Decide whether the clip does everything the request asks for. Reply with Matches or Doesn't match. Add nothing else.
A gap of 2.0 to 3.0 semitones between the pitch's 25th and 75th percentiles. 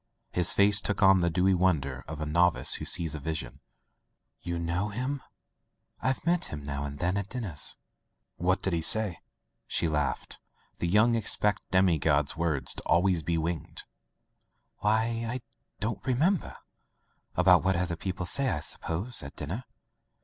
Doesn't match